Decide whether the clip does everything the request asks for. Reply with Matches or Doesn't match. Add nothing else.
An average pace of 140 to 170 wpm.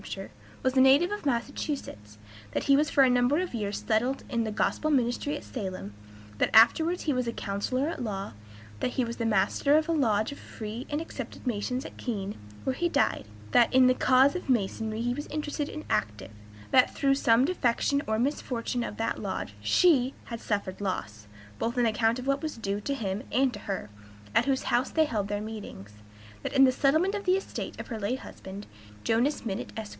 Doesn't match